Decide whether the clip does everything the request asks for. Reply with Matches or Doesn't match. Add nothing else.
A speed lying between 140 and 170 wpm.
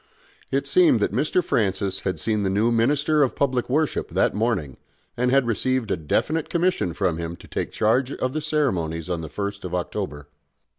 Doesn't match